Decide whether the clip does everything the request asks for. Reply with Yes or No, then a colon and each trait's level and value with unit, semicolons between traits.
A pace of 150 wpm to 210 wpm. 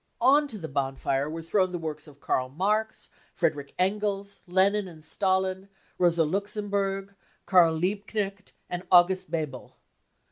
No: slow, 135 wpm